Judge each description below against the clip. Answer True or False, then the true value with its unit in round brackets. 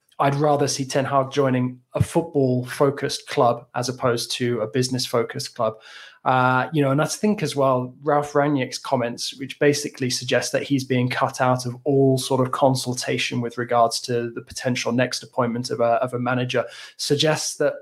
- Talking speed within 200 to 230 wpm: False (185 wpm)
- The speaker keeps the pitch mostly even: True (2.2 semitones)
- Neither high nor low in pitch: False (130 Hz)